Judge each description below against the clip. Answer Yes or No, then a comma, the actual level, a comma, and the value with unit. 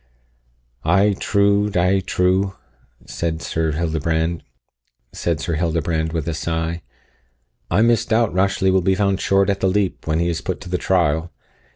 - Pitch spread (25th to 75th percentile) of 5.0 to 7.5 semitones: No, average, 3.1 semitones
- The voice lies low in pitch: Yes, very low, 90 Hz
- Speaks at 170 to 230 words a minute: No, average, 140 wpm